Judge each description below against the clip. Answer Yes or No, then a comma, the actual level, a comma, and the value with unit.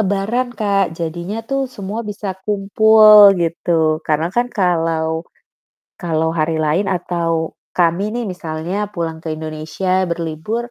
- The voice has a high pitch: No, medium, 175 Hz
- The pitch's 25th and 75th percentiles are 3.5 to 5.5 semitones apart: Yes, average, 4.0 semitones